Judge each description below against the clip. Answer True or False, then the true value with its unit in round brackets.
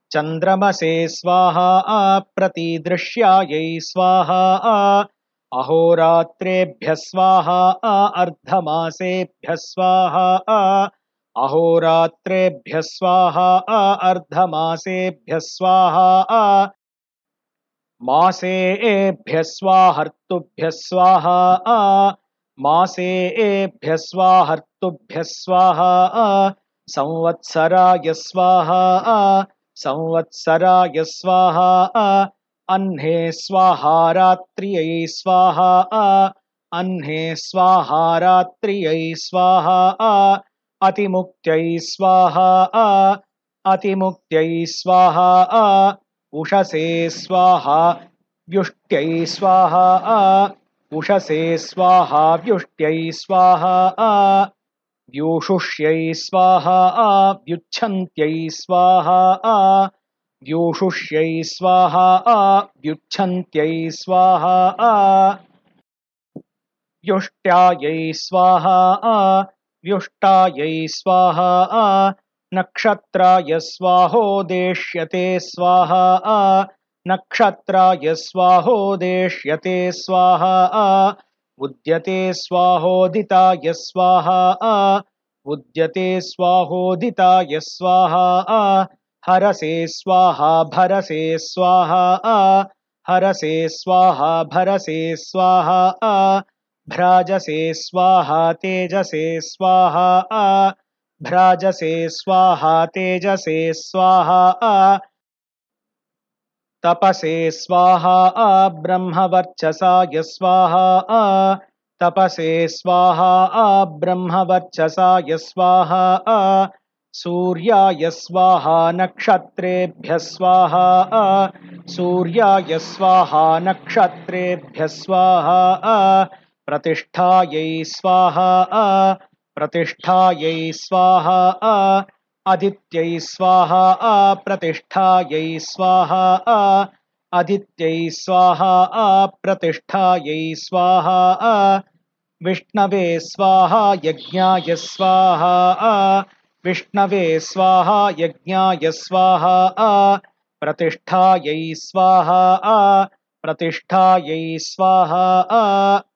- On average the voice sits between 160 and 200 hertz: True (185 Hz)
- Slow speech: True (55 wpm)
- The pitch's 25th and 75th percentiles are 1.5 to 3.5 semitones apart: True (2.4 semitones)